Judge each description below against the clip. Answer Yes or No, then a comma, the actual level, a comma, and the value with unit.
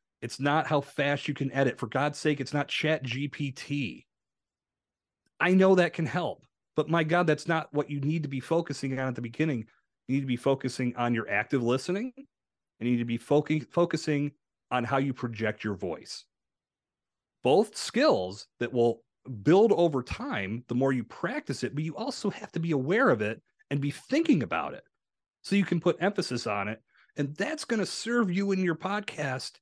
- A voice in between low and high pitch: Yes, medium, 145 Hz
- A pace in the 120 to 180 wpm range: No, average, 200 wpm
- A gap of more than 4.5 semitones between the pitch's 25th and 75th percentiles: Yes, average, 5.2 semitones